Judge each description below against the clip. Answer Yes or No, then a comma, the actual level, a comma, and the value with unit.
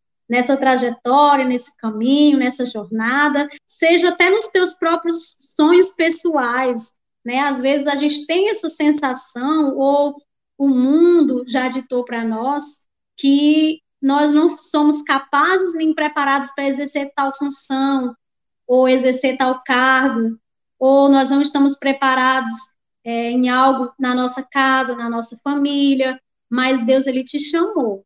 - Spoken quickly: No, average, 135 wpm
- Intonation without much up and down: Yes, narrow, 2.3 semitones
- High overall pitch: Yes, very high, 275 Hz